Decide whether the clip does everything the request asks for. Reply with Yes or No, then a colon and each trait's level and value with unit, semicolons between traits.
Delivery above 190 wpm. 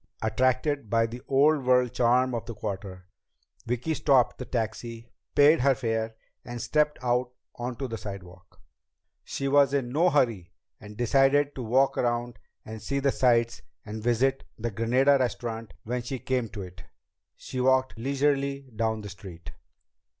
No: average, 155 wpm